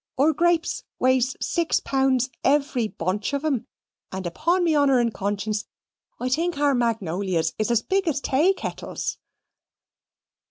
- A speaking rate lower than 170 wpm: Yes, slow, 135 wpm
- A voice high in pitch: Yes, very high, 260 Hz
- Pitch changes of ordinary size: No, wide, 6.1 semitones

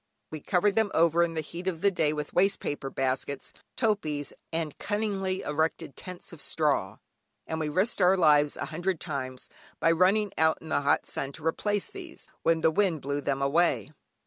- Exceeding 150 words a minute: Yes, average, 190 wpm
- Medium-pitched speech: Yes, medium, 160 Hz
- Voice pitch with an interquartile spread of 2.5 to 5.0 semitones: Yes, average, 4.2 semitones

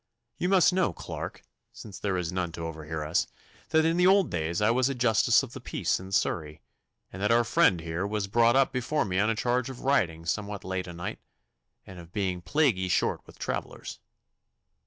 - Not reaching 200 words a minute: No, fast, 205 wpm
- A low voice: Yes, low, 100 Hz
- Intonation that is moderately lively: No, wide, 6.3 semitones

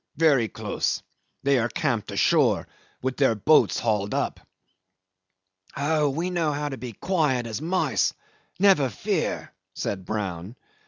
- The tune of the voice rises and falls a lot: Yes, wide, 5.7 semitones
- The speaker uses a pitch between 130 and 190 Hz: Yes, low, 135 Hz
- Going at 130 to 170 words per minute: Yes, average, 140 wpm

